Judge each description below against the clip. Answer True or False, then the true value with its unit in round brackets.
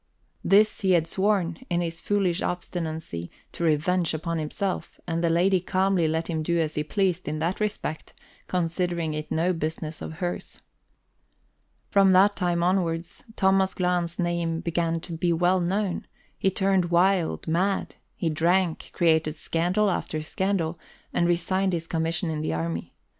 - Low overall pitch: False (175 Hz)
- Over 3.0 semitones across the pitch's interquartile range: False (2.5 semitones)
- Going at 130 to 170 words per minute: True (155 wpm)